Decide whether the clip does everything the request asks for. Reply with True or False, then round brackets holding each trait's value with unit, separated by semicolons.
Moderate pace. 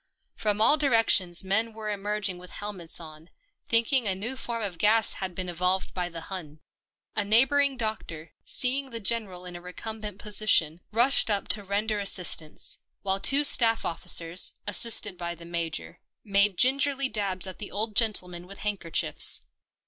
True (165 wpm)